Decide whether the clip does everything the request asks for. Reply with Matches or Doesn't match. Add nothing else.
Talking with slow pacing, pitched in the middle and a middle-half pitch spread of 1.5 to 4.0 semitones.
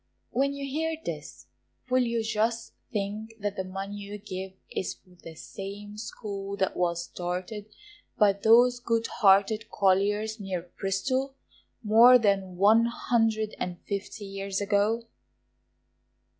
Doesn't match